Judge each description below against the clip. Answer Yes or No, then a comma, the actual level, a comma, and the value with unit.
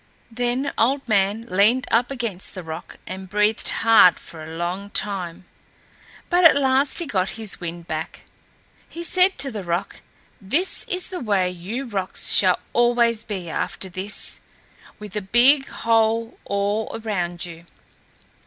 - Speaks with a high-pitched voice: Yes, high, 210 Hz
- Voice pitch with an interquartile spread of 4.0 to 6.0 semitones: Yes, average, 4.7 semitones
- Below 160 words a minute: Yes, average, 150 wpm